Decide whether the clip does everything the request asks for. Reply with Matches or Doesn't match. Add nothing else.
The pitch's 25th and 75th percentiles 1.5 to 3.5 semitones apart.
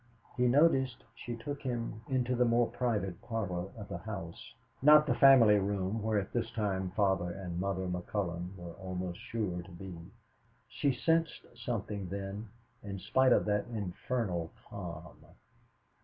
Doesn't match